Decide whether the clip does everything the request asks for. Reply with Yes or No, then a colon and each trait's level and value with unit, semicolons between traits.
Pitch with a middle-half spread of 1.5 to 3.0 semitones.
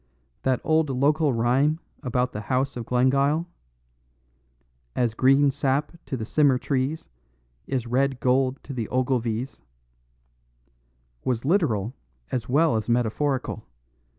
Yes: narrow, 2.5 semitones